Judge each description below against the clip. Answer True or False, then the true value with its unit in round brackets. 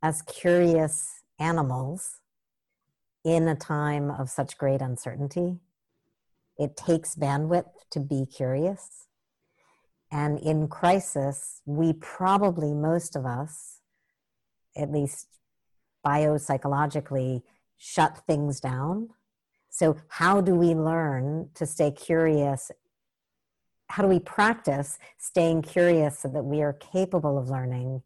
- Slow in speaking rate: True (110 wpm)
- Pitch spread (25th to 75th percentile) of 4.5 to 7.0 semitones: False (3.4 semitones)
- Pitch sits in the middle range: True (155 Hz)